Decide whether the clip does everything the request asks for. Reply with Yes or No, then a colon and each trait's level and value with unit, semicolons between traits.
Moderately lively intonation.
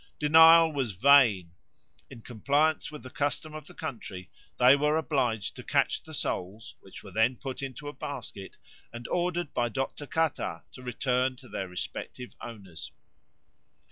Yes: average, 5.0 semitones